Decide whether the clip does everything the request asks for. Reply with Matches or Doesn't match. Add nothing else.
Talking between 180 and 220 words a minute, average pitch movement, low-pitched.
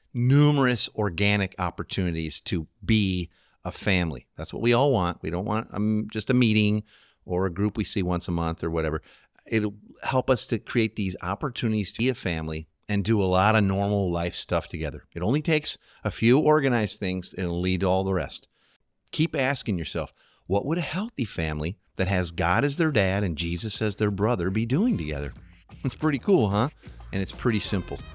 Matches